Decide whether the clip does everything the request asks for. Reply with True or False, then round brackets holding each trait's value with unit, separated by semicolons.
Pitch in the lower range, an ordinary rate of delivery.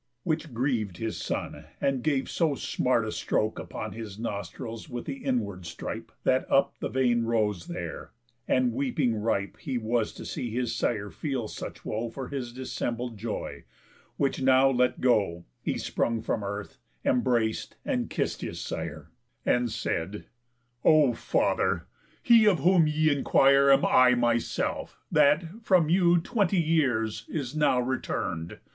True (125 Hz; 150 wpm)